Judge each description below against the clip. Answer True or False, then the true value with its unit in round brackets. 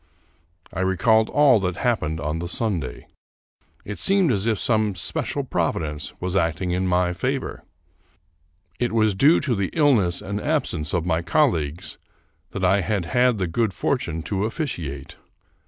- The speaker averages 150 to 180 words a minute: True (155 wpm)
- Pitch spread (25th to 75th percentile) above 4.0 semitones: True (5.4 semitones)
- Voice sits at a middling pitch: False (95 Hz)